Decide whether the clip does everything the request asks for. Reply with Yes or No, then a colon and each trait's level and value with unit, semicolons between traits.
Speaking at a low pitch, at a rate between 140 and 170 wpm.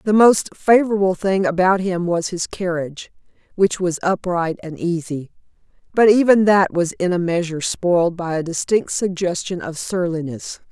No: medium, 180 Hz; average, 155 wpm